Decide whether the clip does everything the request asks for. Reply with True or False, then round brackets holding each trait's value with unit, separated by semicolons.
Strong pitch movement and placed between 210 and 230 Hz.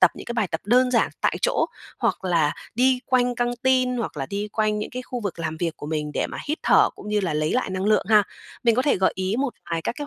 True (6.2 semitones; 215 Hz)